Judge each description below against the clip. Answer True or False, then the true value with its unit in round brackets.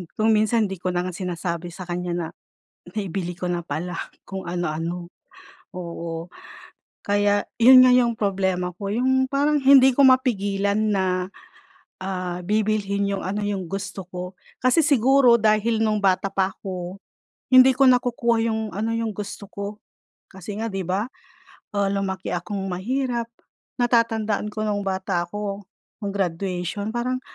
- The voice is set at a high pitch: True (200 Hz)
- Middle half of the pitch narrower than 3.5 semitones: False (3.8 semitones)